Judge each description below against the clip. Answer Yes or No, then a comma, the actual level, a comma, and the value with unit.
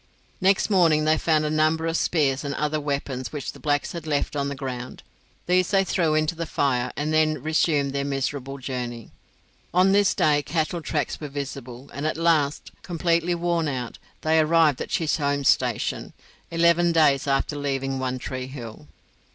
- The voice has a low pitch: No, medium, 150 Hz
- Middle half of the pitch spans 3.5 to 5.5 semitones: No, average, 3.1 semitones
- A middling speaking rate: Yes, average, 175 wpm